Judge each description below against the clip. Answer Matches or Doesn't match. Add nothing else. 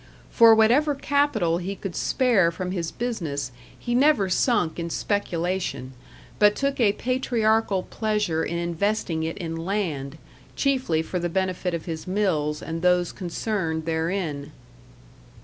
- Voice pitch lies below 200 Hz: Matches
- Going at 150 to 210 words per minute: Doesn't match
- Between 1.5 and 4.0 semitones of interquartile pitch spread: Doesn't match